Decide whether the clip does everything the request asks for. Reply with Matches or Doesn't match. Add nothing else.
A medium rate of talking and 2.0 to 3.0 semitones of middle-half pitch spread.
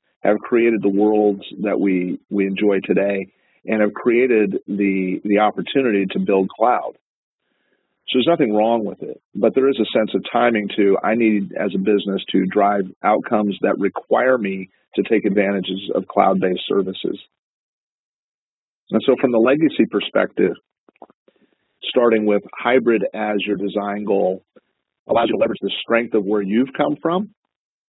Matches